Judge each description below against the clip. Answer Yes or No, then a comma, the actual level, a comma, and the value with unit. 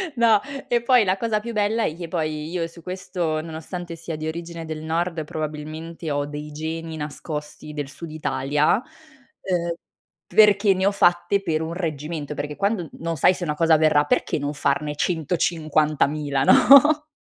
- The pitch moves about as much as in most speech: Yes, average, 3.4 semitones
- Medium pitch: Yes, medium, 165 Hz